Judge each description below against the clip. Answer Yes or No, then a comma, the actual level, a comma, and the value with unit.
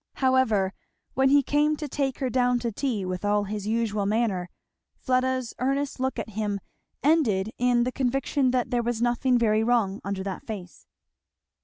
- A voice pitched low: No, high, 240 Hz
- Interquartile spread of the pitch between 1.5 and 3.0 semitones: No, average, 3.9 semitones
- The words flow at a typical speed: Yes, average, 170 wpm